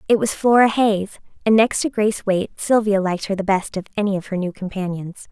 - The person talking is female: Yes, female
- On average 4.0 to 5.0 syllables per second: No, 6.0 syllables/s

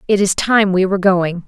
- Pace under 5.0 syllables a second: No, 5.3 syllables/s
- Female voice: Yes, female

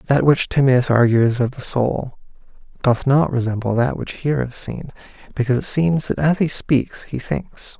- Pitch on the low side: Yes, low, 130 Hz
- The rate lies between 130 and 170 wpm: No, average, 185 wpm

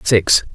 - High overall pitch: No, low, 100 Hz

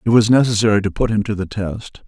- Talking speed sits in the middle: No, fast, 260 wpm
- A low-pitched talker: Yes, low, 105 Hz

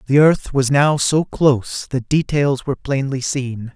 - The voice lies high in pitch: No, low, 135 Hz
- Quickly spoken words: No, average, 175 wpm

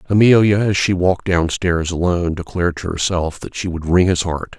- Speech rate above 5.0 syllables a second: Yes, 5.5 syllables/s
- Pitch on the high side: No, very low, 90 Hz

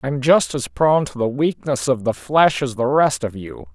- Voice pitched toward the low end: Yes, low, 130 Hz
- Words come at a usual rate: No, fast, 240 wpm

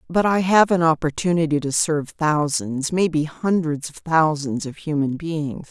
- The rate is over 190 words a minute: No, average, 145 wpm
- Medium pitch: Yes, medium, 155 Hz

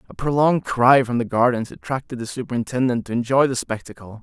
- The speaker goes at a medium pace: Yes, average, 185 wpm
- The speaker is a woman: No, male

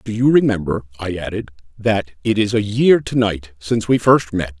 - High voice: No, low, 105 Hz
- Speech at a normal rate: No, fast, 210 wpm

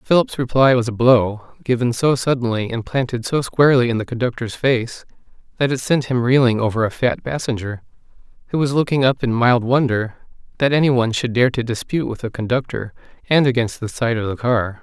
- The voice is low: Yes, low, 120 Hz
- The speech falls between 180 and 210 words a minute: Yes, average, 200 wpm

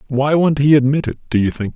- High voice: No, medium, 140 Hz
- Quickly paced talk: Yes, fast, 275 wpm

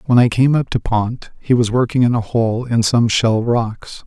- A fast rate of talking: Yes, fast, 235 wpm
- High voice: No, low, 120 Hz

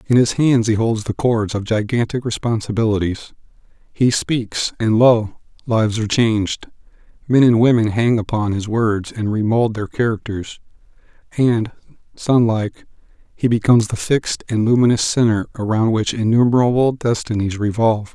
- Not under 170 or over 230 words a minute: No, average, 140 wpm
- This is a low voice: Yes, low, 110 Hz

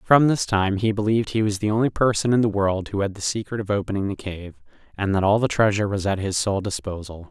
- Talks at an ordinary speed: No, fast, 255 wpm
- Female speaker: No, male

